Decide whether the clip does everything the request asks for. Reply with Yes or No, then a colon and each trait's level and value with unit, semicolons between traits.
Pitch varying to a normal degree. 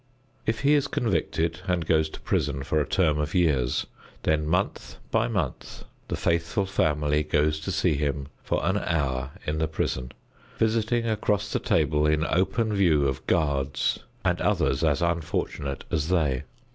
Yes: average, 4.4 semitones